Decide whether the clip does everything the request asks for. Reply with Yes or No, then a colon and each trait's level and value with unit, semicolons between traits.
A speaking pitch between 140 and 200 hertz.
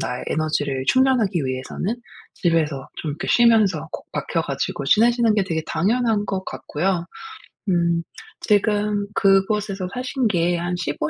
Yes: high, 190 Hz